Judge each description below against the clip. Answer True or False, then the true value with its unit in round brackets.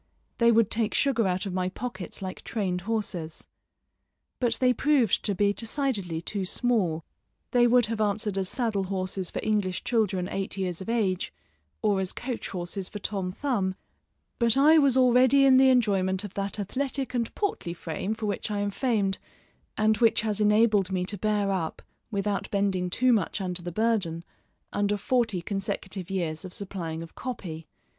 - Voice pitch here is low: False (205 Hz)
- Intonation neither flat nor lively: True (3.8 semitones)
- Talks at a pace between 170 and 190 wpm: True (175 wpm)